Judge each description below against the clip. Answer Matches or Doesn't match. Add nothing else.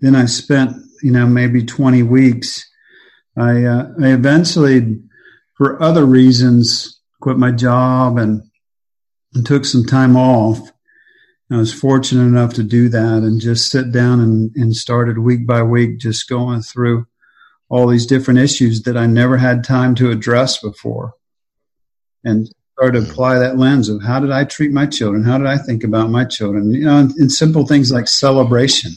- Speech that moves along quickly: Doesn't match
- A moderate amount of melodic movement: Doesn't match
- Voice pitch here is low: Matches